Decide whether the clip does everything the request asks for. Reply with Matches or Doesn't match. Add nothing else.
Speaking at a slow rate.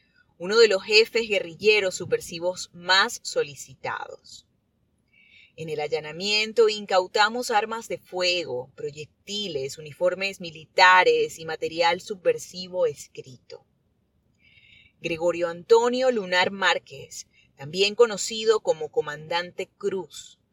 Matches